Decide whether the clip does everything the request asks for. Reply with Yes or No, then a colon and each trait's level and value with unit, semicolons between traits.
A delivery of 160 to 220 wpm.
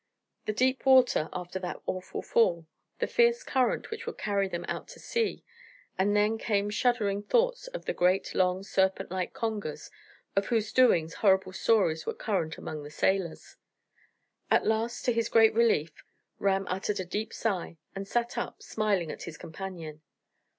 Yes: average, 165 wpm